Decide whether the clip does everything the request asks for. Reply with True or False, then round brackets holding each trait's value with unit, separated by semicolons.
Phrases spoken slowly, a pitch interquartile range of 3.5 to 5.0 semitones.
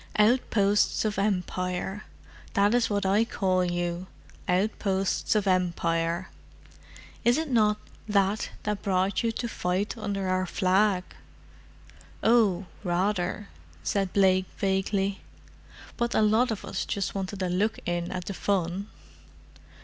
False (125 wpm; 2.4 semitones)